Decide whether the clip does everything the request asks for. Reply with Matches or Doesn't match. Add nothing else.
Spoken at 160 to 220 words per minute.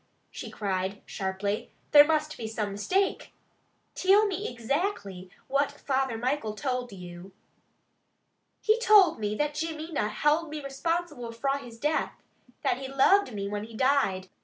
Doesn't match